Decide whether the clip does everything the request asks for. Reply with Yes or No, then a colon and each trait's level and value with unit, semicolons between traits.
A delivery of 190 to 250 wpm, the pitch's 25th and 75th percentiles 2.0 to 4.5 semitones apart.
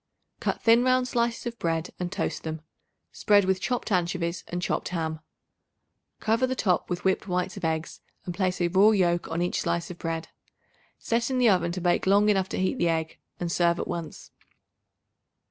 Yes: average, 195 wpm; average, 3.6 semitones